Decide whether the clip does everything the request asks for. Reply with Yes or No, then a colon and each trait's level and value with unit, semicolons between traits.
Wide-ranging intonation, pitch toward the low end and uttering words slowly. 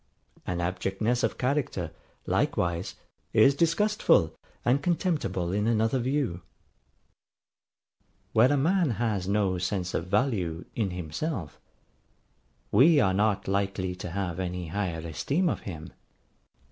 Yes: wide, 6.7 semitones; low, 100 Hz; slow, 120 wpm